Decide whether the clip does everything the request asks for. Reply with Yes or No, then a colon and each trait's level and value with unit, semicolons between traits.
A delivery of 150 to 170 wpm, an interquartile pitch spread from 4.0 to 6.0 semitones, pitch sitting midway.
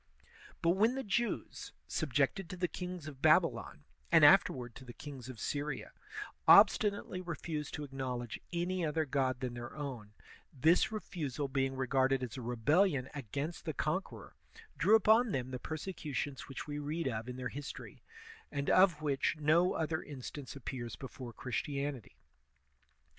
Yes: average, 155 wpm; average, 4.6 semitones; medium, 145 Hz